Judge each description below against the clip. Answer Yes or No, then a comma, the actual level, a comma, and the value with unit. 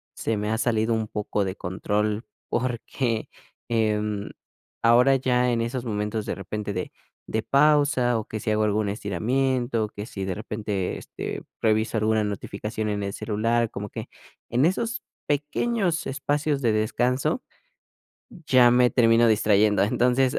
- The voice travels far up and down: No, average, 3.1 semitones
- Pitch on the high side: No, low, 110 Hz